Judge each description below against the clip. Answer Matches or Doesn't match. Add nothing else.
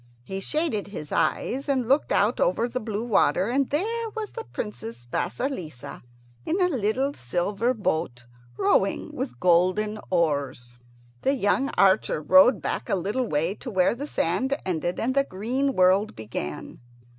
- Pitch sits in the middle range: Doesn't match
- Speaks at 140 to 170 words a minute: Matches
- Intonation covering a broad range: Matches